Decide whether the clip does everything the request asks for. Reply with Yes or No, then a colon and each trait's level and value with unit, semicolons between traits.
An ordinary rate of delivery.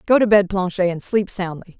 No: fast, 235 wpm